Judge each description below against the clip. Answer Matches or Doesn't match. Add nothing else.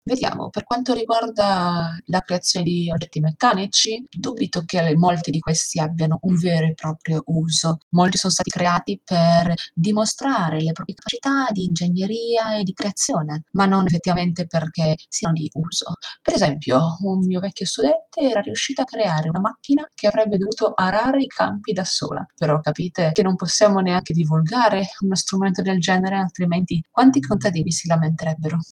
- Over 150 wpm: Matches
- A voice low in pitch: Doesn't match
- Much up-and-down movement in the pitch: Doesn't match